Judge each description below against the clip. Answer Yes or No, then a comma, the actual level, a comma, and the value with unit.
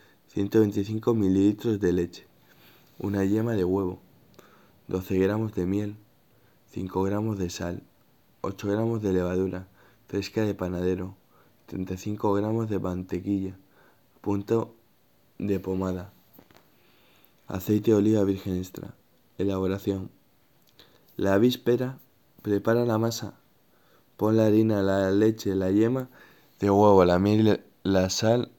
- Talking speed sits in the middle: No, slow, 115 wpm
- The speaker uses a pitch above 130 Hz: No, low, 100 Hz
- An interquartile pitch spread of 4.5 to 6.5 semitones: No, narrow, 2.6 semitones